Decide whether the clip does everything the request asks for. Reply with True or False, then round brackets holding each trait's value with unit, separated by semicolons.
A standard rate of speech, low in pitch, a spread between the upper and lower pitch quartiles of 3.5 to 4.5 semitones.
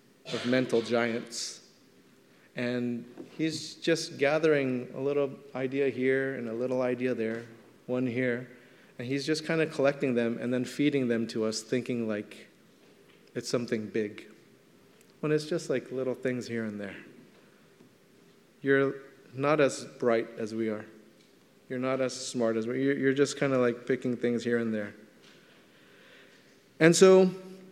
False (155 wpm; 125 Hz; 2.9 semitones)